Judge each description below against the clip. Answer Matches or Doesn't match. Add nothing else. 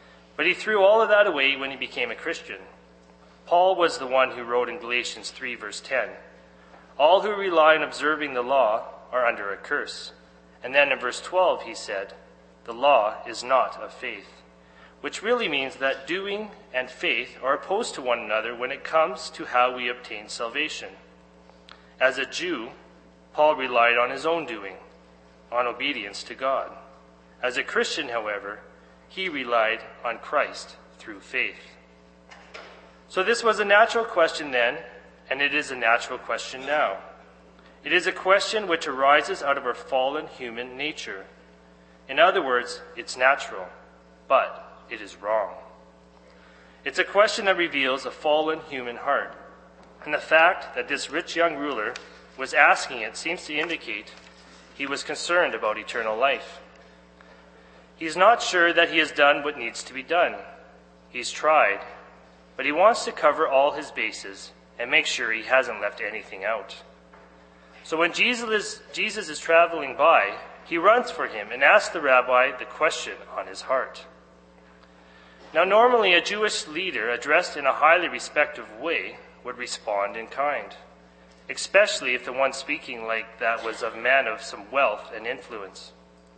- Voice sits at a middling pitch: Doesn't match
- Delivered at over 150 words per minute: Matches